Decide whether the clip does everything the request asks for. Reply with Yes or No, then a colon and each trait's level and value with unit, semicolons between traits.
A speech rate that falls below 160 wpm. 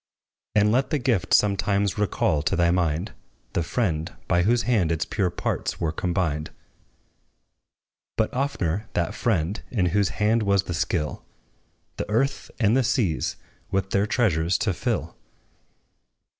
Yes: average, 145 wpm